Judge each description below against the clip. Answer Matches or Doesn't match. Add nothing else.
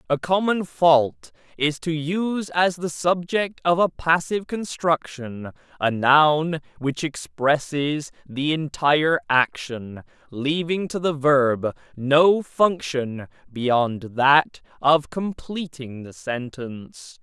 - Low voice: Doesn't match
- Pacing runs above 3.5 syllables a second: Doesn't match